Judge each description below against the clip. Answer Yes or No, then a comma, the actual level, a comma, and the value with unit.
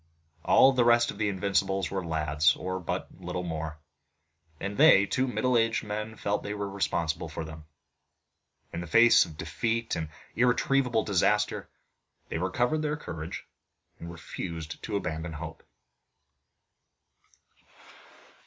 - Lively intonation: Yes, wide, 5.8 semitones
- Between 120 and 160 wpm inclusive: Yes, slow, 135 wpm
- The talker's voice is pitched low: Yes, very low, 95 Hz